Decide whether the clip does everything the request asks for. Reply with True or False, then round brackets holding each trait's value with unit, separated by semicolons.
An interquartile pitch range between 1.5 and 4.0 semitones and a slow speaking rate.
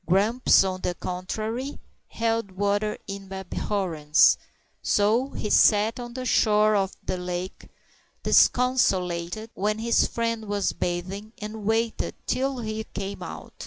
True (3.1 semitones; 125 wpm)